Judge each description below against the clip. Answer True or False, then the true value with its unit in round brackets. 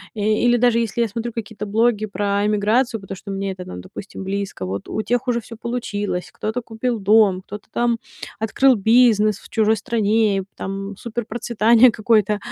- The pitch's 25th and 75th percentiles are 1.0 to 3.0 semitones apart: True (2.7 semitones)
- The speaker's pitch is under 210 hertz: False (215 Hz)